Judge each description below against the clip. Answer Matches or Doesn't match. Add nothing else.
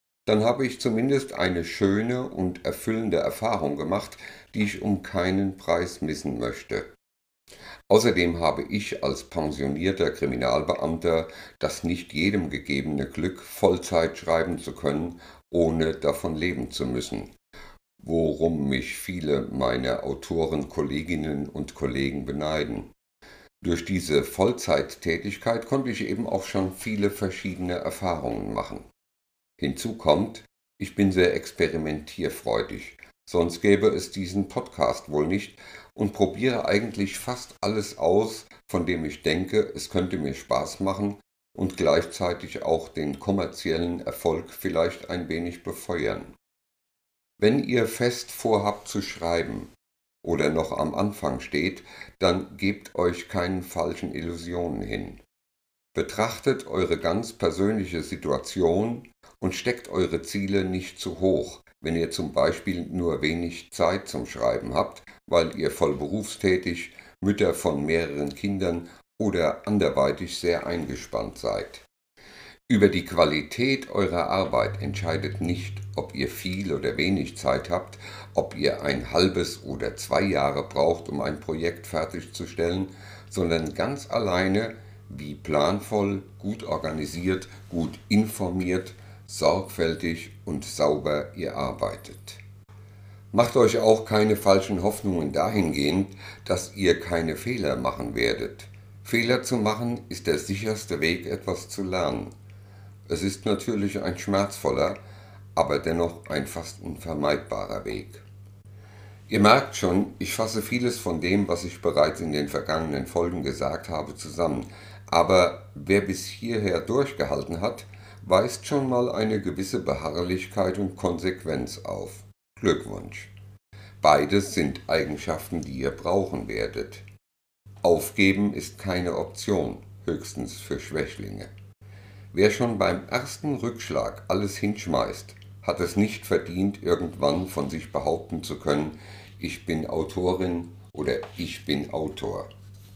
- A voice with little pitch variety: Doesn't match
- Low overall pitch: Matches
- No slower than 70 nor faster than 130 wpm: Matches